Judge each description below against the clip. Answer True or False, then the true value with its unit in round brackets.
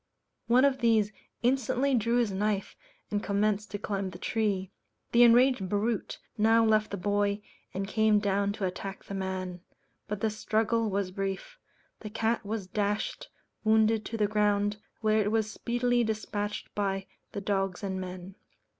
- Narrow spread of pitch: True (2.1 semitones)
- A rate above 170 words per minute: False (160 wpm)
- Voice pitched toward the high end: True (210 Hz)